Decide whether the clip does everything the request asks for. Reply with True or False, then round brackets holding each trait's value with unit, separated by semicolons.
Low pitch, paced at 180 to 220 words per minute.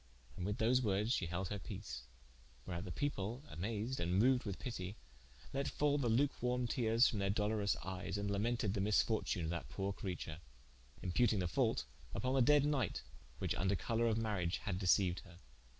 True (105 Hz; 185 wpm)